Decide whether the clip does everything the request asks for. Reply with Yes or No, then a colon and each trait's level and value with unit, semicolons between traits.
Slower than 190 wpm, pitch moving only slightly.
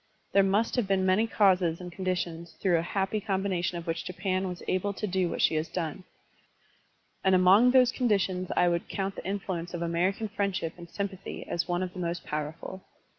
No: average, 200 wpm; narrow, 2.3 semitones